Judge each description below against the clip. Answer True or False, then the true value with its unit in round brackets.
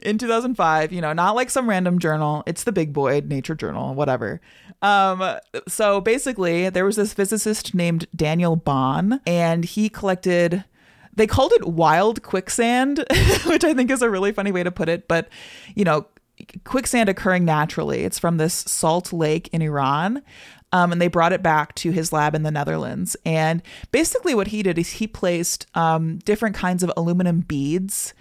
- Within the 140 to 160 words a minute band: False (180 wpm)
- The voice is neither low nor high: True (180 Hz)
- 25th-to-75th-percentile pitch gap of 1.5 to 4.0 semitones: False (4.4 semitones)